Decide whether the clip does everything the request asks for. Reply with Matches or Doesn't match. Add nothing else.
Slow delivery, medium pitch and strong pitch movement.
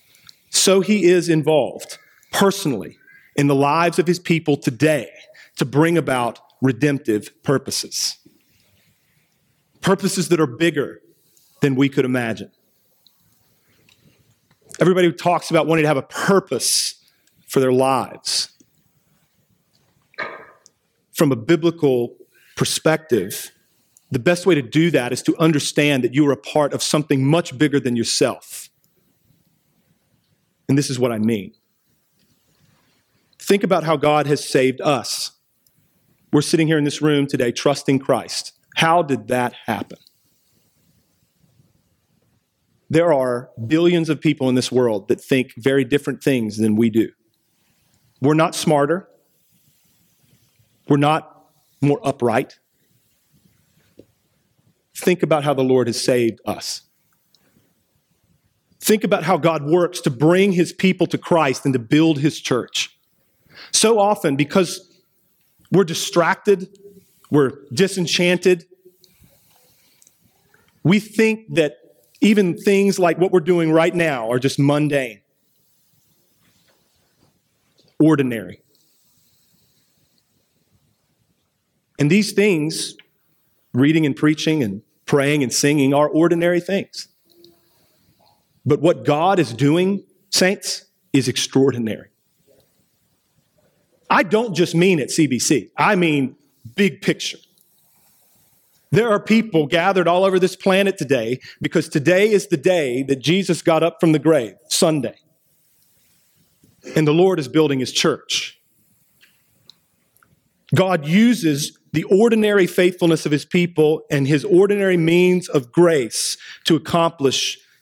Doesn't match